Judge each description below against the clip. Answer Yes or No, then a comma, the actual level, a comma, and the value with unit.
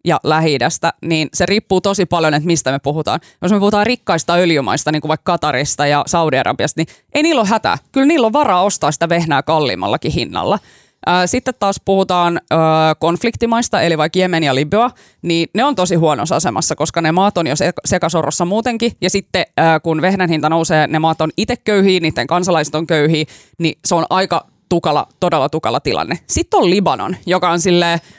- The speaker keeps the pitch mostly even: No, average, 3.5 semitones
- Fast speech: Yes, fast, 185 wpm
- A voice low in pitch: No, medium, 170 Hz